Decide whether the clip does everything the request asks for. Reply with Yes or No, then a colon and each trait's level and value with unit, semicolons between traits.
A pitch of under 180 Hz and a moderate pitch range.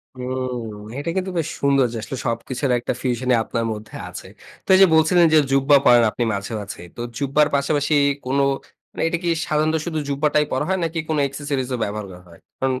Yes: low, 135 Hz; average, 4.2 semitones